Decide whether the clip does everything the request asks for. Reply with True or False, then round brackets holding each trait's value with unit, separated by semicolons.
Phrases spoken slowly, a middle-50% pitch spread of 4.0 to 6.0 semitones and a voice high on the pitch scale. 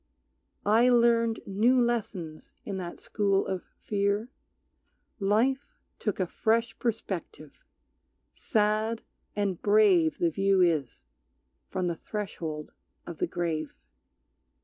True (105 wpm; 4.3 semitones; 200 Hz)